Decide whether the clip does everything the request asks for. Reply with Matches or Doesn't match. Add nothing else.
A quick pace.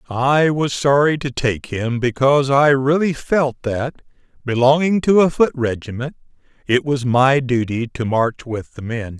Doesn't match